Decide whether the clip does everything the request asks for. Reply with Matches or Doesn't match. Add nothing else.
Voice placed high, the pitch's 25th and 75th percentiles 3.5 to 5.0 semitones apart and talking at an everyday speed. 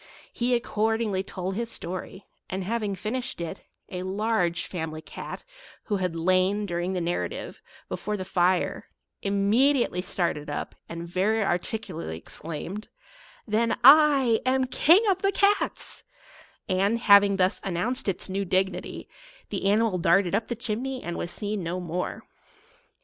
Matches